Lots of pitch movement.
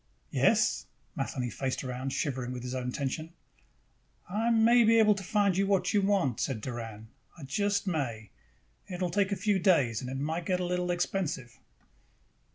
Yes: wide, 7.5 semitones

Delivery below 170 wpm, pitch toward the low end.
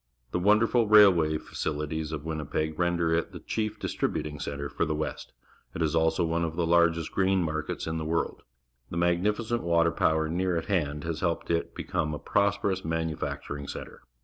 No: average, 200 wpm; very low, 85 Hz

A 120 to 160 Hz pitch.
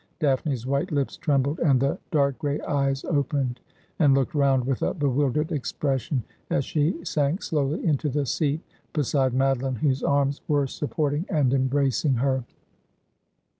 Yes: medium, 140 Hz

